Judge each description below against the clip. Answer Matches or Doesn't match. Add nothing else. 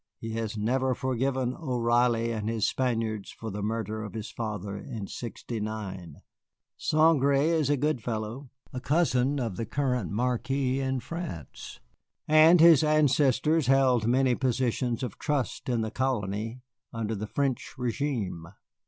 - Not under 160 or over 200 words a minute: Doesn't match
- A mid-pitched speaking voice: Doesn't match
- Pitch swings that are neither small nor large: Matches